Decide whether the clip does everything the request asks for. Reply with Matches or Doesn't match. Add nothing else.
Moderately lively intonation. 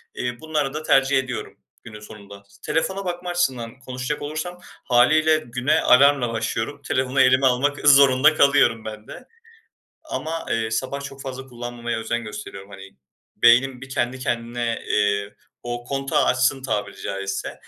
Matches